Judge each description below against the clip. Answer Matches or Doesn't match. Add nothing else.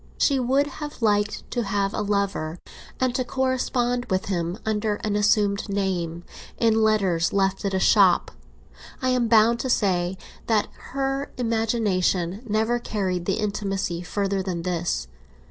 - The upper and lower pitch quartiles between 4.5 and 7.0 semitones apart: Doesn't match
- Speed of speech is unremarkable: Matches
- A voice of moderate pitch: Doesn't match